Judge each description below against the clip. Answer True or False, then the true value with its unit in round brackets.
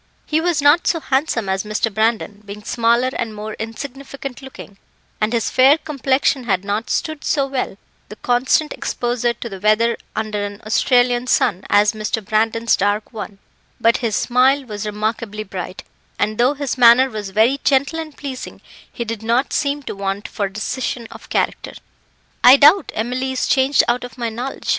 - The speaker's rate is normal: True (175 wpm)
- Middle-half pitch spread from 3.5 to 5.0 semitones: True (3.8 semitones)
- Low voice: False (235 Hz)